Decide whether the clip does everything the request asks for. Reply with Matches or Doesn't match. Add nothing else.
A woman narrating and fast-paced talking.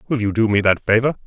Doesn't match